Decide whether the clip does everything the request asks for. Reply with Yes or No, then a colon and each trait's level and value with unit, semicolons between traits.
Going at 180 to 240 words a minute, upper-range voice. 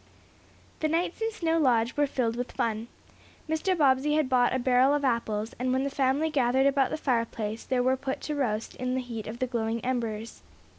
Yes: fast, 205 wpm; very high, 255 Hz